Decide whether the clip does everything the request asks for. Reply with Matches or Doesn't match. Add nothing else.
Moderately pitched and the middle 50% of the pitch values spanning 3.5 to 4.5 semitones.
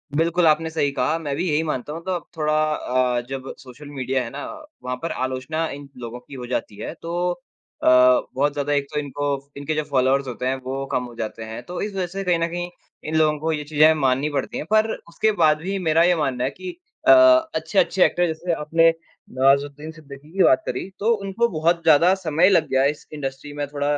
Matches